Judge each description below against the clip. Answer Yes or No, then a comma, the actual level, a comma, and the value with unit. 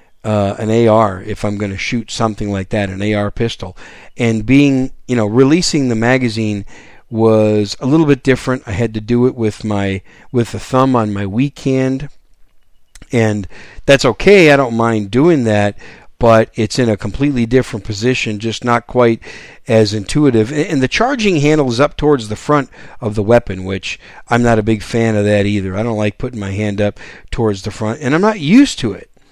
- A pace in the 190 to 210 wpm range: Yes, average, 200 wpm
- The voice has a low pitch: Yes, low, 115 Hz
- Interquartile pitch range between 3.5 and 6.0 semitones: Yes, average, 3.8 semitones